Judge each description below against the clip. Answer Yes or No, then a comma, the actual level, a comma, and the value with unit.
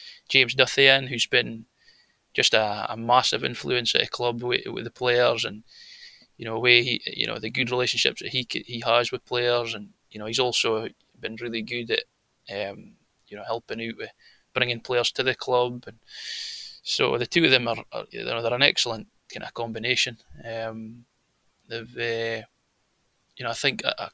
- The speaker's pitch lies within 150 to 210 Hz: No, low, 120 Hz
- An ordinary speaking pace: Yes, average, 190 wpm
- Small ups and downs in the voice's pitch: Yes, narrow, 1.5 semitones